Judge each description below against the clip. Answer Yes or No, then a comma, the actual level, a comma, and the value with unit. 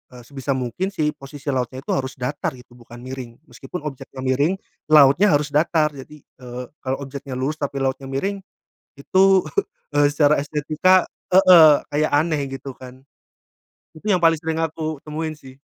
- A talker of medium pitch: Yes, medium, 145 Hz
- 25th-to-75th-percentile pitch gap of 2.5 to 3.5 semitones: Yes, average, 2.9 semitones